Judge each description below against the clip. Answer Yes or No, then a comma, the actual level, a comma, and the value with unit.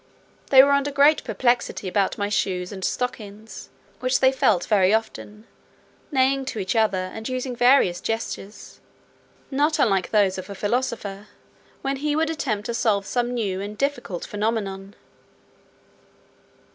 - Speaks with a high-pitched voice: Yes, high, 220 Hz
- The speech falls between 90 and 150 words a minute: Yes, average, 145 wpm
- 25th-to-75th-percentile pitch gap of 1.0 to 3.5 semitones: No, average, 4.7 semitones